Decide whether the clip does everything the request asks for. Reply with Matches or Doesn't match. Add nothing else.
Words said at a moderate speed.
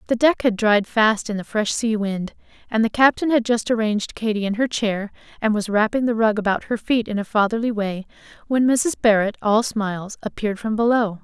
Doesn't match